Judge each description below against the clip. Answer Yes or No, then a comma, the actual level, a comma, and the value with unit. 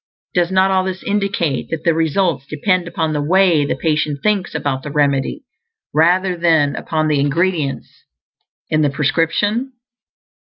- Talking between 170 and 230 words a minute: No, average, 150 wpm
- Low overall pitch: No, medium, 165 Hz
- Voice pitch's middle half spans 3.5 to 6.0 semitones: Yes, average, 4.1 semitones